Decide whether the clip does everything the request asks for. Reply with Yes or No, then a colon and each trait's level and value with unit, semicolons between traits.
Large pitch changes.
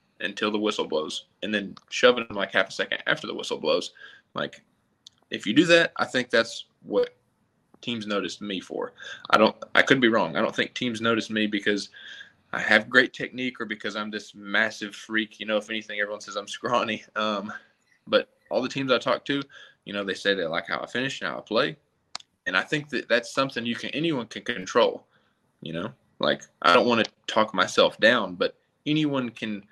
Yes: wide, 6.6 semitones